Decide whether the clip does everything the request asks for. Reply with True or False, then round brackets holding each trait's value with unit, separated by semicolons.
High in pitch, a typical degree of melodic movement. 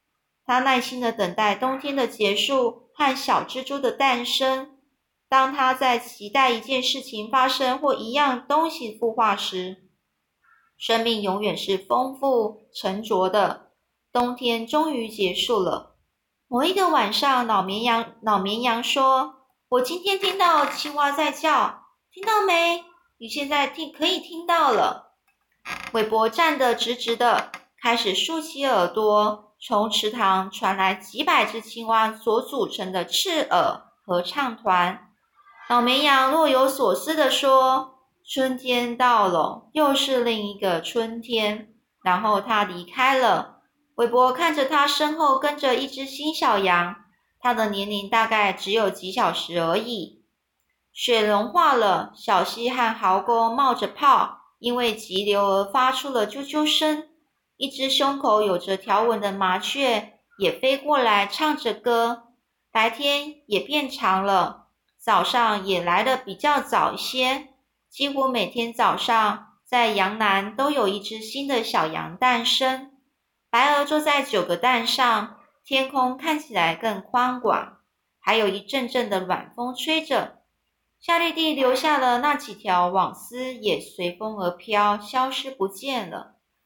True (245 Hz; 4.5 semitones)